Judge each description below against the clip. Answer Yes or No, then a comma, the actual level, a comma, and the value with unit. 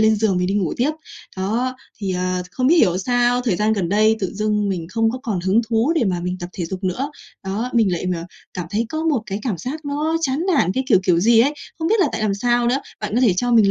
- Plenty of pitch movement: No, average, 4.8 semitones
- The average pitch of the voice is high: Yes, high, 220 Hz